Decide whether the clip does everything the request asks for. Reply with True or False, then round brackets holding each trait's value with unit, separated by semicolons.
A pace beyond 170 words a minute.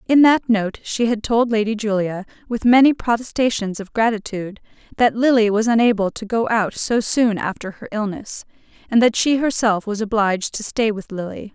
True (180 wpm)